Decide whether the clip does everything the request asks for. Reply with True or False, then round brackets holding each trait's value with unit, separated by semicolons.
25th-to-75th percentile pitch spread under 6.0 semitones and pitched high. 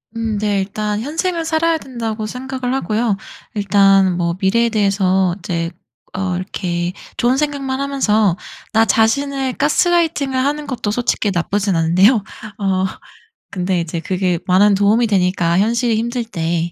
True (5.5 semitones; 210 Hz)